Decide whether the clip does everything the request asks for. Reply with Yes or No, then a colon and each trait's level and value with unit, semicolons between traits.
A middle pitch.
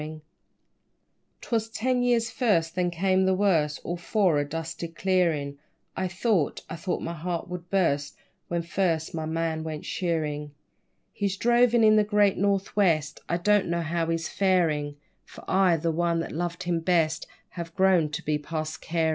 Yes: medium, 170 Hz